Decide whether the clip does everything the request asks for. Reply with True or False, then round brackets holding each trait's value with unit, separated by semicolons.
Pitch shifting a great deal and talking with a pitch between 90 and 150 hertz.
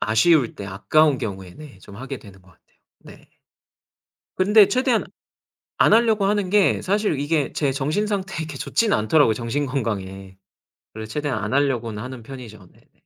True (9.0 semitones; 135 Hz)